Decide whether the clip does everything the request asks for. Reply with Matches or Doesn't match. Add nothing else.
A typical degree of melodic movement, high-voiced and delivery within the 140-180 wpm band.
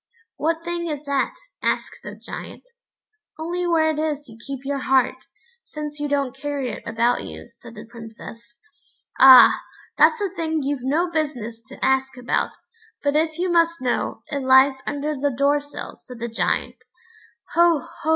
Matches